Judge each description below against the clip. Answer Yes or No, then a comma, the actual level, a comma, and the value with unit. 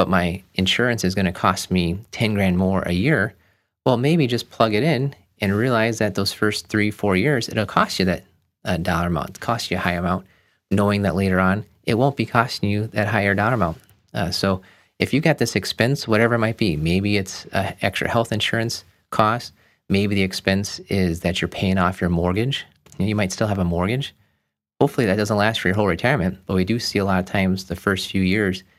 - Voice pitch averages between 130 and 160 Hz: No, low, 100 Hz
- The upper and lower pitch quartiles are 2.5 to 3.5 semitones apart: Yes, average, 3.1 semitones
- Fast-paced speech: Yes, fast, 220 wpm